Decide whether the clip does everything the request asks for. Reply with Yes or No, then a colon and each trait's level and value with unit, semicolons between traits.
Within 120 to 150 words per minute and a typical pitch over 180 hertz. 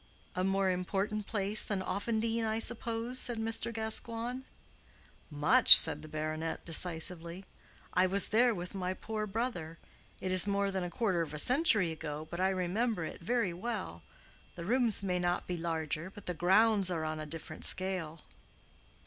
No: average, 165 wpm; high, 190 Hz